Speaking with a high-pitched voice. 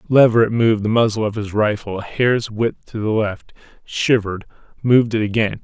No: low, 110 Hz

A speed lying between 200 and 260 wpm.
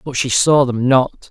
Yes: fast, 230 wpm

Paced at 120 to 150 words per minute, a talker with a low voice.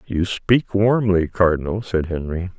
Yes: average, 140 wpm; very low, 95 Hz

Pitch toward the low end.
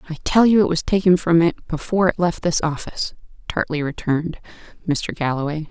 No: medium, 165 Hz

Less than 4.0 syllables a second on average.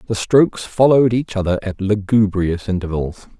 No: 5.2 syllables/s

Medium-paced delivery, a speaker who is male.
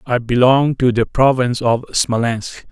Yes: average, 155 wpm; male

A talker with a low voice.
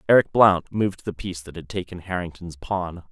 Yes: very low, 90 Hz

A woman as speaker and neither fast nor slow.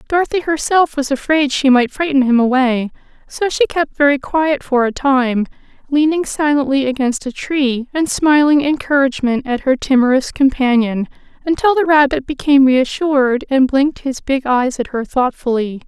Yes: female; average, 160 wpm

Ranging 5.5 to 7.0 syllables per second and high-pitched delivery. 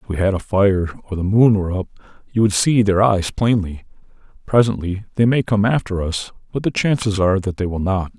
No: 5.7 syllables/s; low, 100 Hz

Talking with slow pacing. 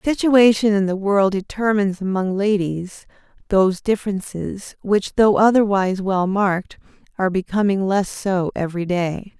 Yes: slow, 130 wpm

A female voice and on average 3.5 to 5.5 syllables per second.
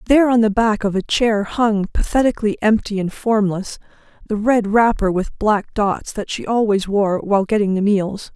Yes: female; 4.9 syllables/s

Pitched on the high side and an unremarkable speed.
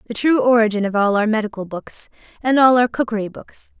Yes: high, 225 Hz; average, 190 wpm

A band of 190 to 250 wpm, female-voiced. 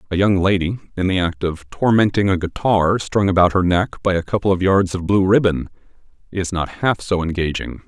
No: fast, 205 wpm; male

